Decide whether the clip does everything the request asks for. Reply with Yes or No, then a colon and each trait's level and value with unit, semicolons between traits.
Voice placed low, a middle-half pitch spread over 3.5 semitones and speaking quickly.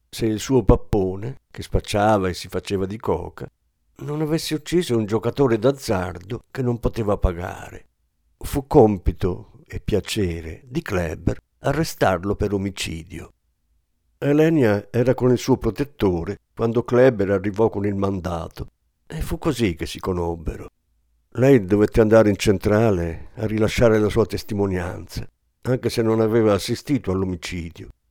No: low, 105 Hz; average, 4.5 semitones; average, 135 wpm